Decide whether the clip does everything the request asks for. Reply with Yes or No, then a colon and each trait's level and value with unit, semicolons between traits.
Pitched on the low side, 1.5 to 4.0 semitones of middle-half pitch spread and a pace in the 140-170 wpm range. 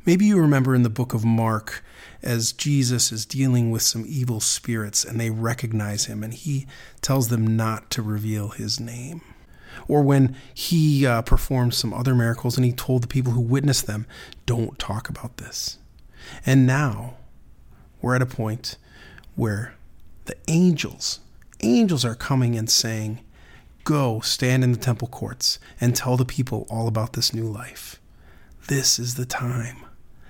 Yes: low, 120 Hz; average, 2.9 semitones; average, 160 wpm